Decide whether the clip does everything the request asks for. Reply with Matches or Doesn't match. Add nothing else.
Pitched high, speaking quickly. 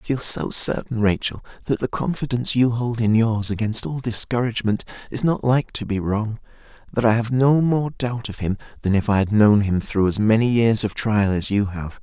Doesn't match